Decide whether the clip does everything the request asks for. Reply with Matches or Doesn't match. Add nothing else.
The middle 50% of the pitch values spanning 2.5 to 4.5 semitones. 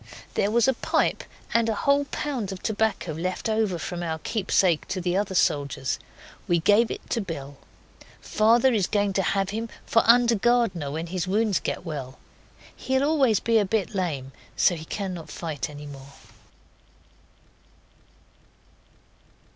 Doesn't match